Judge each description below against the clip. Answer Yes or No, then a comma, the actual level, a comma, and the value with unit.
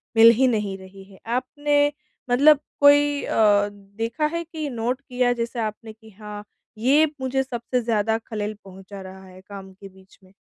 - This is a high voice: Yes, high, 225 Hz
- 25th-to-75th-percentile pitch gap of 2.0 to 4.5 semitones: No, average, 4.9 semitones